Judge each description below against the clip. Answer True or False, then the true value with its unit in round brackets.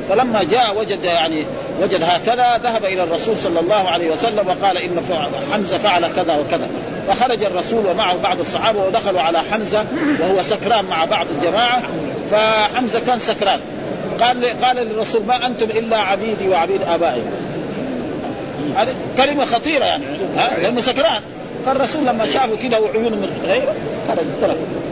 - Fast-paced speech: True (145 wpm)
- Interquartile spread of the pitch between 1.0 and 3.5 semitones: False (3.9 semitones)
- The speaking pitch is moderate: False (220 Hz)